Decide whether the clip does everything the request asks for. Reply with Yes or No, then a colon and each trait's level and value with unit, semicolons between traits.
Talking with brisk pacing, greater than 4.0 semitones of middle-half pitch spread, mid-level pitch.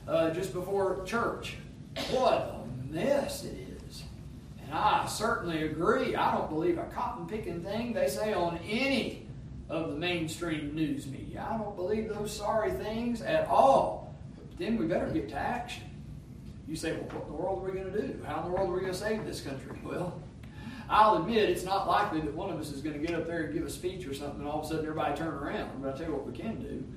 Yes: fast, 235 wpm; average, 5.2 semitones; medium, 180 Hz